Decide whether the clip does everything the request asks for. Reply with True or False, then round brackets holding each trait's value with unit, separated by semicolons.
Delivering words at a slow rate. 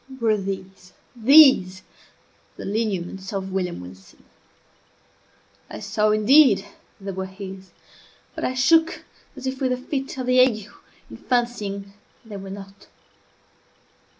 True (130 wpm)